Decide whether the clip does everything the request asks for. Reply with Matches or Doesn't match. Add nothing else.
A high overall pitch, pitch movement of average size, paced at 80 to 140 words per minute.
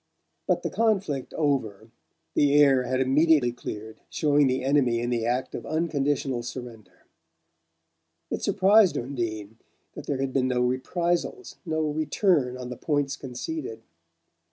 Doesn't match